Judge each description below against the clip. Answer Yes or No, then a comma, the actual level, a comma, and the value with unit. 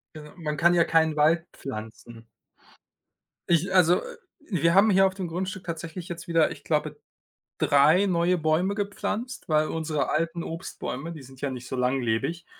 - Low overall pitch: No, medium, 165 Hz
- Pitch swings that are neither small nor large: Yes, average, 3.2 semitones